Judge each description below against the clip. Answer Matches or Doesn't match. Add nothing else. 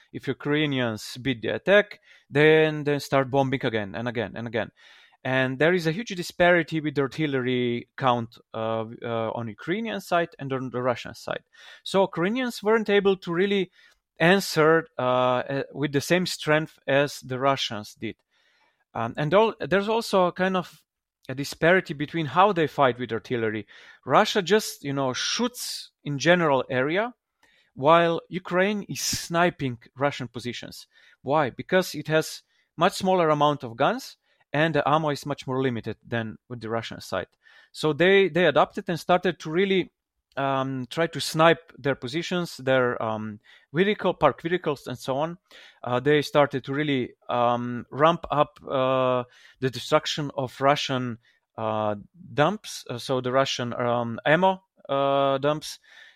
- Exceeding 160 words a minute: Doesn't match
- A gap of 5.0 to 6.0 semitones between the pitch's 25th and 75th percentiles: Matches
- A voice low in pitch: Doesn't match